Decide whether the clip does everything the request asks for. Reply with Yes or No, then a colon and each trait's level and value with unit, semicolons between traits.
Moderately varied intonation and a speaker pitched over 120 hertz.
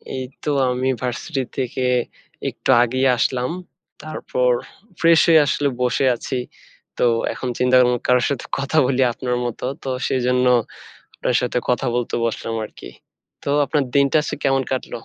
No: narrow, 1.8 semitones; low, 130 Hz